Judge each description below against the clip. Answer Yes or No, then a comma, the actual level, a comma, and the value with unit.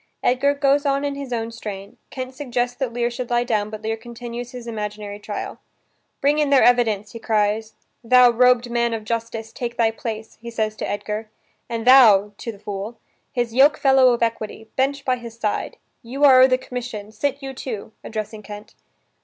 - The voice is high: Yes, high, 235 Hz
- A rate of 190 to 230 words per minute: Yes, average, 195 wpm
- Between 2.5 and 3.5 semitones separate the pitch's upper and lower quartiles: Yes, average, 2.8 semitones